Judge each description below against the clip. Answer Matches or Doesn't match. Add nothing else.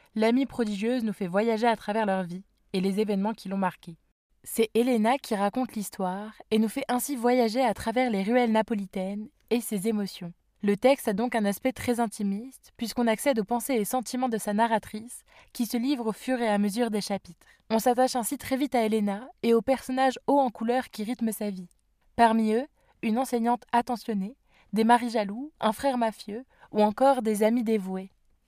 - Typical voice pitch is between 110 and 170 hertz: Doesn't match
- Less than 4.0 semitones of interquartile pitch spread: Matches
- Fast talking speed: Doesn't match